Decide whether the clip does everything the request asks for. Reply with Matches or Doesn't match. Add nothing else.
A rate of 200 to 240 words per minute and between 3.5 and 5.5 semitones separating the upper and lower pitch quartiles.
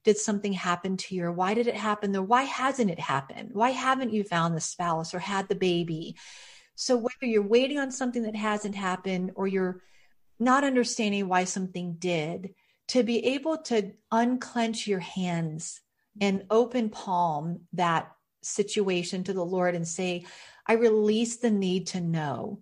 Doesn't match